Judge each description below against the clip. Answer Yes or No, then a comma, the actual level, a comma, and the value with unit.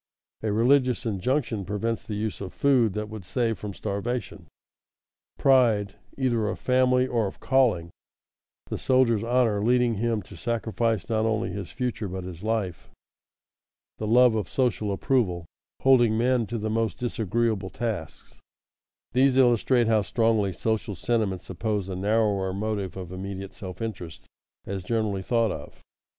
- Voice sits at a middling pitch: No, low, 110 Hz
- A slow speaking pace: No, average, 145 wpm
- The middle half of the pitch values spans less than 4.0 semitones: Yes, average, 3.3 semitones